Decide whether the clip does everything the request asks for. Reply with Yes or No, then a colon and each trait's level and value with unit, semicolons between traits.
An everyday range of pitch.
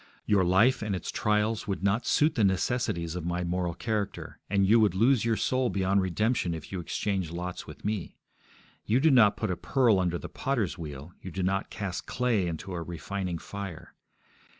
Yes: average, 3.7 semitones